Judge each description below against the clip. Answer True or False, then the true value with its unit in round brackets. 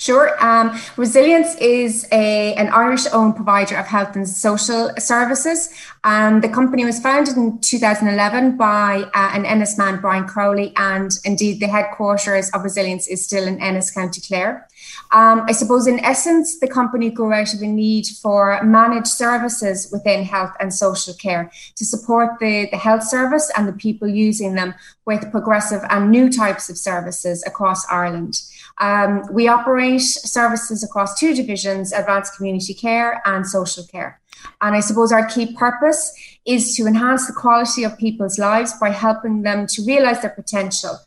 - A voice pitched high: True (215 Hz)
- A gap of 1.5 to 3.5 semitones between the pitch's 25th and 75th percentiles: True (3.1 semitones)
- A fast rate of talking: False (165 wpm)